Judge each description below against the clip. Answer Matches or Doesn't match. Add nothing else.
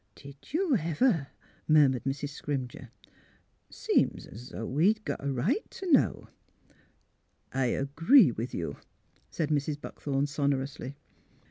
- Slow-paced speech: Matches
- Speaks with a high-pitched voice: Doesn't match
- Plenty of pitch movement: Doesn't match